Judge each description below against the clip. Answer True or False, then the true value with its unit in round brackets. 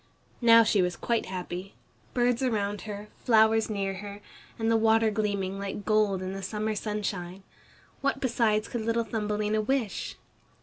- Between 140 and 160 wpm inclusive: True (150 wpm)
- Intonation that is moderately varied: False (2.1 semitones)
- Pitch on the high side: True (215 Hz)